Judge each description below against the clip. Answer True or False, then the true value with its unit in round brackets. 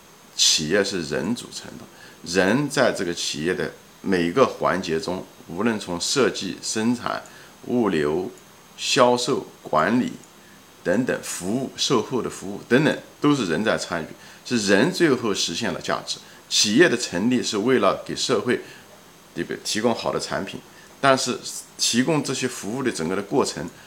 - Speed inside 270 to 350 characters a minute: False (230 characters per minute)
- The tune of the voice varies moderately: False (7.3 semitones)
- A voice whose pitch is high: False (125 Hz)